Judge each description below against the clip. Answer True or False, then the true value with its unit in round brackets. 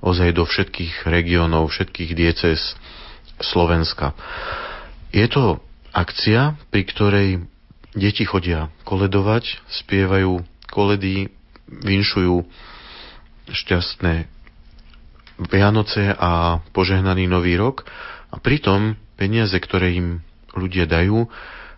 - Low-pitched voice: True (95 Hz)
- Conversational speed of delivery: False (85 wpm)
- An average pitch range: True (3.1 semitones)